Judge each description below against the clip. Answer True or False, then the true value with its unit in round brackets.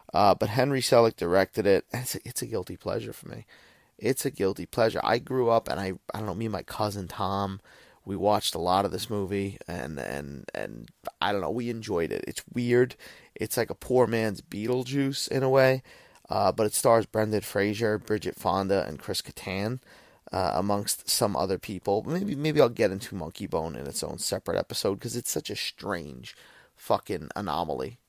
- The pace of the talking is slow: False (200 wpm)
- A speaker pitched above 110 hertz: False (105 Hz)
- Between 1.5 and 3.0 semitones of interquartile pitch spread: False (3.6 semitones)